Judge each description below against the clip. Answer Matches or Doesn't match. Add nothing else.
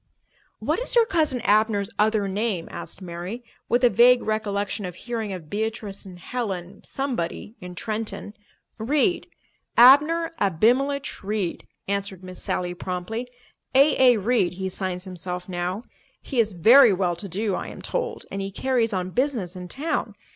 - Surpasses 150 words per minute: Doesn't match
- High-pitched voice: Matches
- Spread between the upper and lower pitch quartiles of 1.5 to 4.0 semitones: Doesn't match